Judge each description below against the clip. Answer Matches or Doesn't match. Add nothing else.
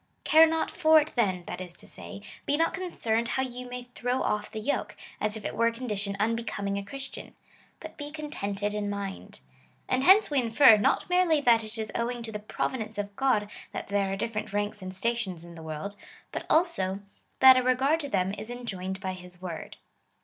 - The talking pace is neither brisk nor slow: Doesn't match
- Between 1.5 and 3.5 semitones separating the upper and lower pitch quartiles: Doesn't match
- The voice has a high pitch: Matches